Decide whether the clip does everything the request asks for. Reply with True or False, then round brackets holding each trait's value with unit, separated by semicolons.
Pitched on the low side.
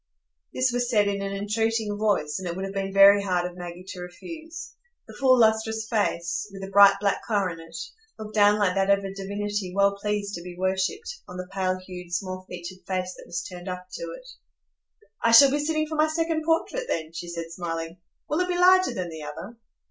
False (200 Hz)